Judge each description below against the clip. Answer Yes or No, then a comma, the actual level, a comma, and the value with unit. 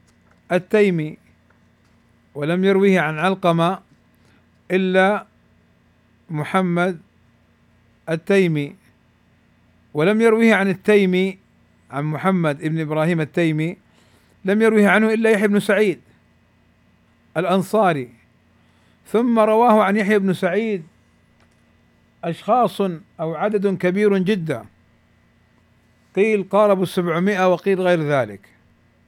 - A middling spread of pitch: No, wide, 9.0 semitones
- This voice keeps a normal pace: Yes, average, 85 wpm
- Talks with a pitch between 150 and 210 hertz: Yes, medium, 165 Hz